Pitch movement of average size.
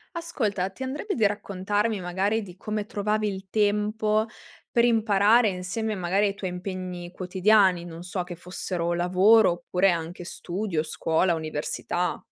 Yes: average, 3.0 semitones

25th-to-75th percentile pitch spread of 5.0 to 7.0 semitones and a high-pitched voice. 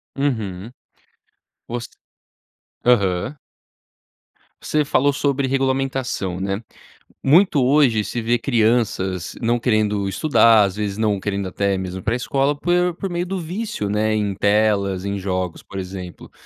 No: wide, 5.5 semitones; low, 110 Hz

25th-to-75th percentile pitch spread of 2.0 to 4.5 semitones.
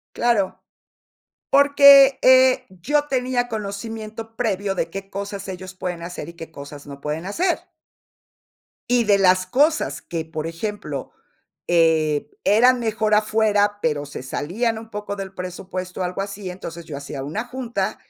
No: average, 5.1 semitones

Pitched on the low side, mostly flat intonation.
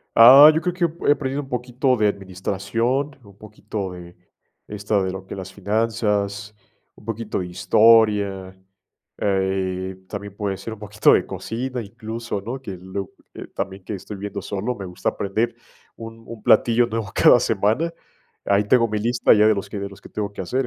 No: low, 105 Hz; average, 3.0 semitones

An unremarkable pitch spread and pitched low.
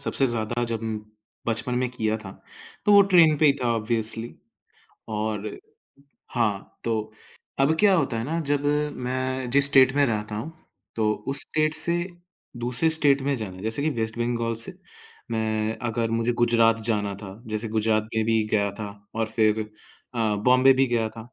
Yes: average, 3.4 semitones; low, 115 Hz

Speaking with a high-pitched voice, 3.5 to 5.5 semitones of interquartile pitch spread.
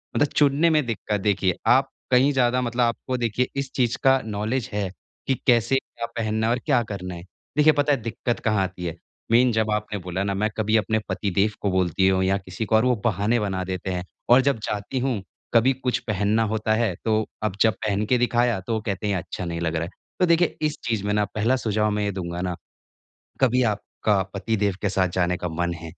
No: low, 110 Hz; average, 4.1 semitones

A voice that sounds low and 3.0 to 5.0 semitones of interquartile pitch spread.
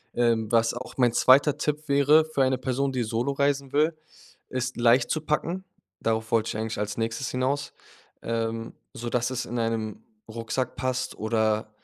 Yes: low, 125 Hz; average, 3.4 semitones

